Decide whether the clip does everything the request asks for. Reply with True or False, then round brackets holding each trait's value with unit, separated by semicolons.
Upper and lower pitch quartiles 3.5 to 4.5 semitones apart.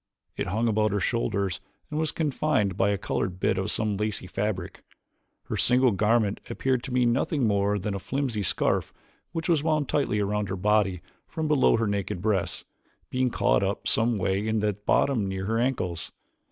True (4.2 semitones)